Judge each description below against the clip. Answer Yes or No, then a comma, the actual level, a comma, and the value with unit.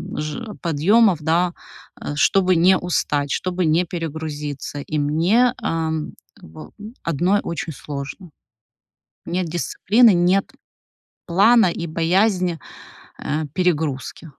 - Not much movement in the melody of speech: No, average, 3.3 semitones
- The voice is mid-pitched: Yes, medium, 170 Hz